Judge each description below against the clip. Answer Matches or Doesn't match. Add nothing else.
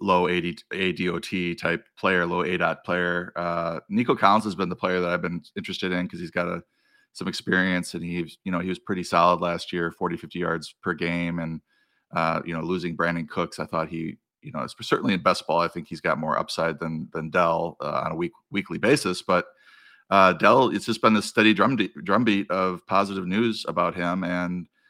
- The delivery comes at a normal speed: Doesn't match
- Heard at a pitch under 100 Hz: Matches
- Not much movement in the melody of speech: Matches